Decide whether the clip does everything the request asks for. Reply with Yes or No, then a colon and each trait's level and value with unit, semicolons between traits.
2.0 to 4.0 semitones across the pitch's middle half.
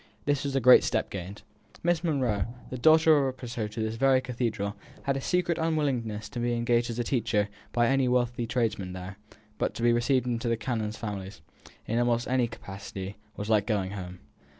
Yes: average, 3.6 semitones